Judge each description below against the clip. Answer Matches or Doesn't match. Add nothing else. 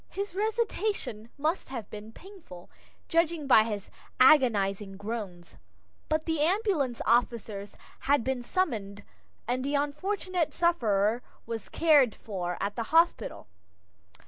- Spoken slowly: Matches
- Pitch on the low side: Doesn't match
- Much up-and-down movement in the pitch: Matches